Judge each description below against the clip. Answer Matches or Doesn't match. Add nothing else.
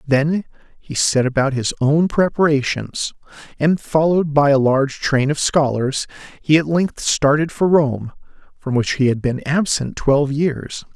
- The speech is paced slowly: Doesn't match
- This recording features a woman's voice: Doesn't match